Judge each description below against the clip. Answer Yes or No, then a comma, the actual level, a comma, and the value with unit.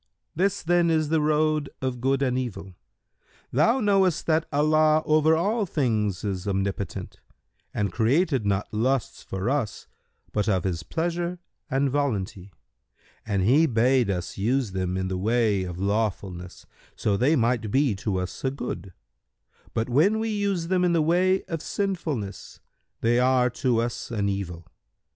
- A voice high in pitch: No, low, 125 Hz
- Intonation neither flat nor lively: No, wide, 7.7 semitones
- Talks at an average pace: Yes, average, 155 wpm